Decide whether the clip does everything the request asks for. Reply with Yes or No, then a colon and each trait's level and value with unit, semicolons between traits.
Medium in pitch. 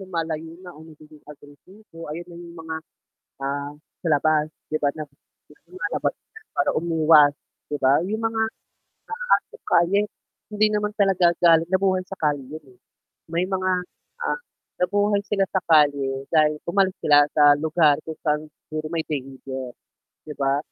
Yes: medium, 160 Hz